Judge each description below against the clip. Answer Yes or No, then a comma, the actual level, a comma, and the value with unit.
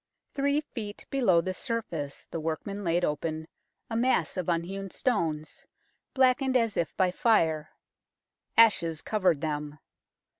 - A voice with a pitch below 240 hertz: Yes, medium, 185 Hz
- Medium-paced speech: No, slow, 125 wpm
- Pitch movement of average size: No, wide, 6.2 semitones